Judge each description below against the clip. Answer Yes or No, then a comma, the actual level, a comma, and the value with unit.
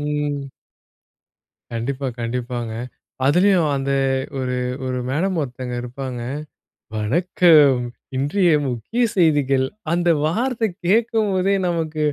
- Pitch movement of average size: No, wide, 5.8 semitones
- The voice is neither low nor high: Yes, medium, 145 Hz